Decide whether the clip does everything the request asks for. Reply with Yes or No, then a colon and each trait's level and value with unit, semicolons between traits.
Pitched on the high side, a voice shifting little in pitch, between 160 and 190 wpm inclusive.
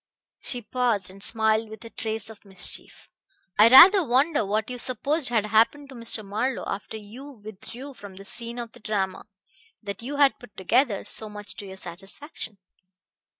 No: high, 220 Hz; average, 3.7 semitones; average, 175 wpm